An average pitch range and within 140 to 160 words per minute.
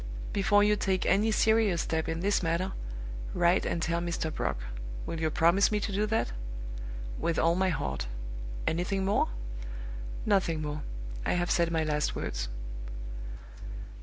Yes: average, 3.6 semitones; average, 150 wpm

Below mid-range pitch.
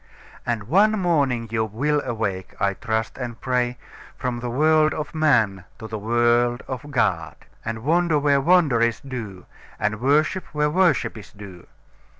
Yes: low, 125 Hz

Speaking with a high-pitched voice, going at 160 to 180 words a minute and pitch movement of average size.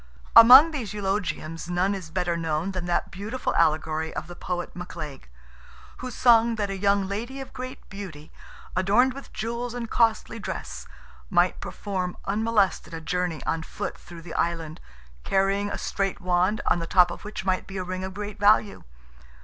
Yes: high, 195 Hz; average, 175 wpm; average, 3.6 semitones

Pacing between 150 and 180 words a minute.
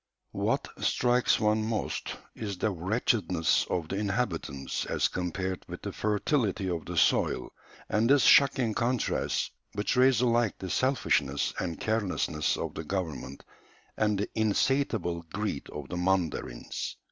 No: slow, 135 wpm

